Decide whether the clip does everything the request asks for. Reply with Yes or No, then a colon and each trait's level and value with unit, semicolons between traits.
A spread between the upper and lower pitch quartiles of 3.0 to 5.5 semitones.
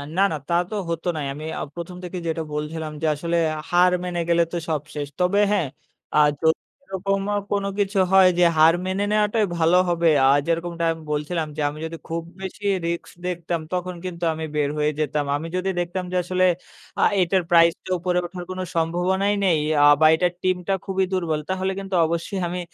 No: narrow, 2.4 semitones